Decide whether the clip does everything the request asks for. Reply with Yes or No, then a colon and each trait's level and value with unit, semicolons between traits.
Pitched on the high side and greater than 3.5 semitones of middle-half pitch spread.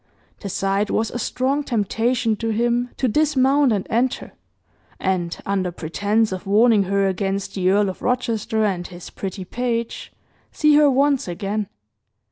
Yes: high, 215 Hz; average, 4.2 semitones